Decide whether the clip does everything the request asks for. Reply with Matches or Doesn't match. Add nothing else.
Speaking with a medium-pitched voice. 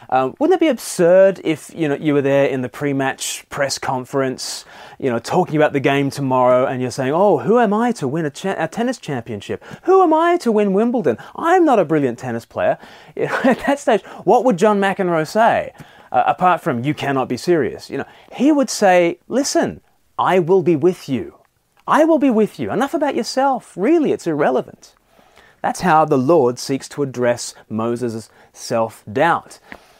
Matches